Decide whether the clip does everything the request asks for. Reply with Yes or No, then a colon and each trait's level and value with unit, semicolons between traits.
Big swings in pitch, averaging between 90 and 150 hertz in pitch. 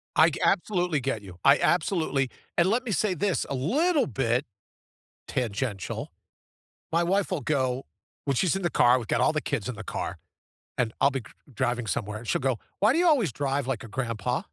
Yes: wide, 6.7 semitones; medium, 140 Hz